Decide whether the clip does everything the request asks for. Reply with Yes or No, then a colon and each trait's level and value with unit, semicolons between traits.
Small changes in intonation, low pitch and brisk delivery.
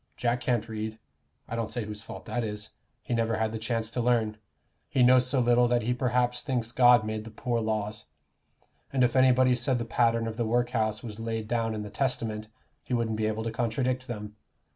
Yes: narrow, 2.0 semitones; low, 115 Hz; fast, 215 wpm